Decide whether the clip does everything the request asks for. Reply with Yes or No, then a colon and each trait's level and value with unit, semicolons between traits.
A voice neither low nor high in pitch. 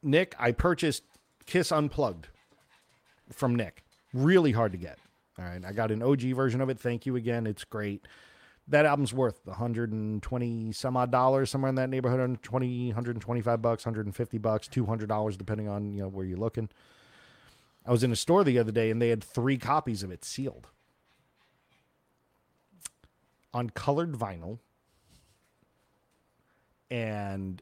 No: low, 120 Hz